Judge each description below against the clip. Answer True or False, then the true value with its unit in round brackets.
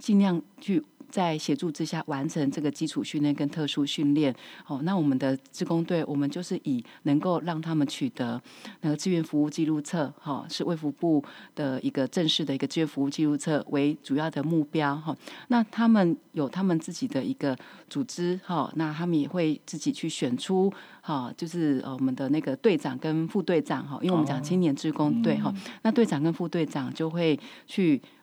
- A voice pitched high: False (160 Hz)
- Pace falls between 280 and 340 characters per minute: True (295 characters per minute)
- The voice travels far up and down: False (3.8 semitones)